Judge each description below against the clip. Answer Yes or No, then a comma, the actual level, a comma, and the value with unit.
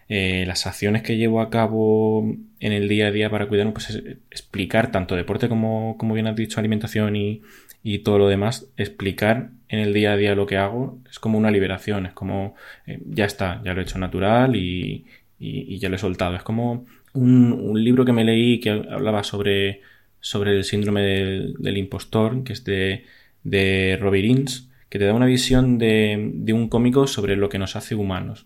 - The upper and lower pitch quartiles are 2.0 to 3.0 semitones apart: Yes, narrow, 2.5 semitones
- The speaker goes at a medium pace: No, fast, 205 wpm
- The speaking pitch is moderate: No, low, 105 Hz